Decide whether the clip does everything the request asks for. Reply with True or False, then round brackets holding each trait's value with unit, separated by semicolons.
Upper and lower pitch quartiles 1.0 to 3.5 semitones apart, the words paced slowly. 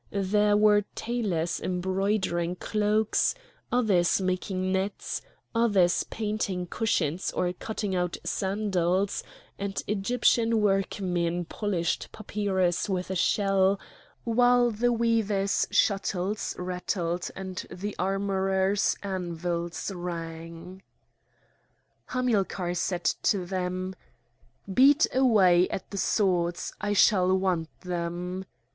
True (2.6 semitones; 95 wpm)